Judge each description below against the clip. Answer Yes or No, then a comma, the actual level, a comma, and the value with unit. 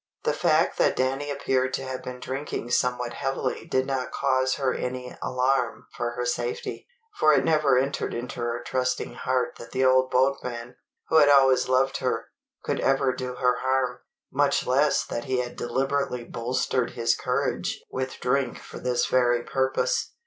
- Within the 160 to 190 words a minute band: Yes, average, 170 wpm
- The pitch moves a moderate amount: No, narrow, 1.3 semitones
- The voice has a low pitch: Yes, low, 130 Hz